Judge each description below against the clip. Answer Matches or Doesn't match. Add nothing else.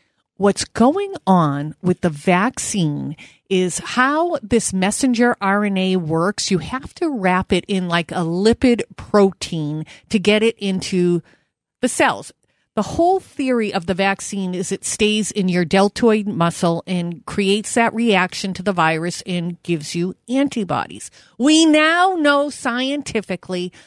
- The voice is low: Doesn't match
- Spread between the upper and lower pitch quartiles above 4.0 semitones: Matches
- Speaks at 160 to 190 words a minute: Doesn't match